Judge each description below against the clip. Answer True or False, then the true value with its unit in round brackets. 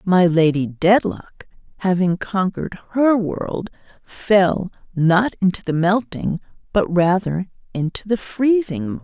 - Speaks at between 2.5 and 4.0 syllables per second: True (3.9 syllables/s)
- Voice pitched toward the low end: False (185 Hz)